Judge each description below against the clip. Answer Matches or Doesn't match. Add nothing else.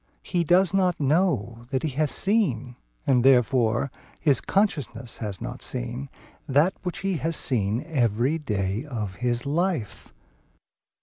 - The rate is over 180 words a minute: Doesn't match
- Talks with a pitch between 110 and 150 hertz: Matches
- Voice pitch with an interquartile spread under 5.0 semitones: Doesn't match